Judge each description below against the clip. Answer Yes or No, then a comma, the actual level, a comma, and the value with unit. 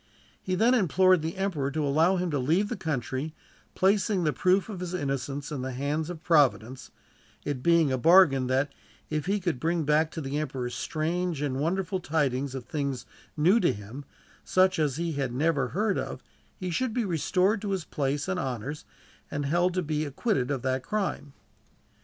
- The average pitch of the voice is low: No, medium, 155 Hz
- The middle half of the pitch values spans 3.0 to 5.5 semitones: Yes, average, 4.9 semitones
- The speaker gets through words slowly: No, average, 190 wpm